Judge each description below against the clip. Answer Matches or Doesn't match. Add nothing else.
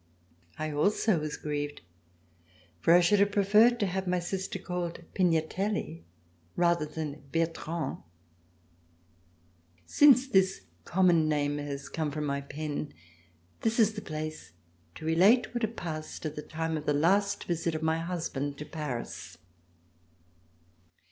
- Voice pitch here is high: Doesn't match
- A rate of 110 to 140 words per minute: Matches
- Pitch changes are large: Doesn't match